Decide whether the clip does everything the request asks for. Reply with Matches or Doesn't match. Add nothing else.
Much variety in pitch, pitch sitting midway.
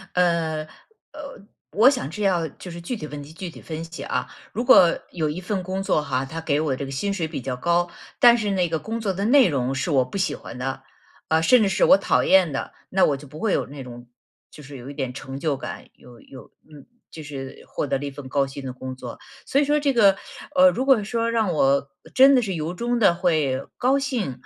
Matches